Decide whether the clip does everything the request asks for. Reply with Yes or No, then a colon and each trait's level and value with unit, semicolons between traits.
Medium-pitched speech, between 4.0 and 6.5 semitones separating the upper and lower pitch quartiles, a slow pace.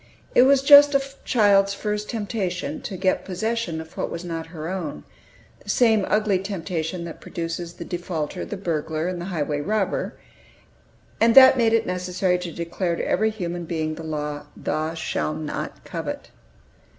No: medium, 180 Hz; average, 4.4 semitones; average, 165 wpm